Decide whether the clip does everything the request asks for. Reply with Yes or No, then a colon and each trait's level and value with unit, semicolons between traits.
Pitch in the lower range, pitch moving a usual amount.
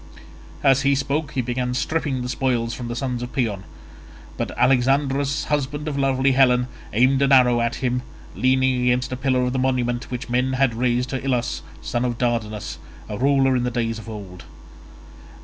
No: low, 125 Hz; narrow, 1.7 semitones